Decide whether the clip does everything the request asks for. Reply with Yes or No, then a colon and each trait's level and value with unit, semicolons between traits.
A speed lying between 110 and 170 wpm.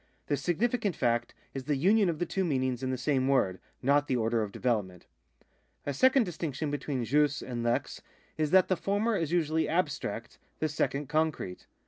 No: average, 180 wpm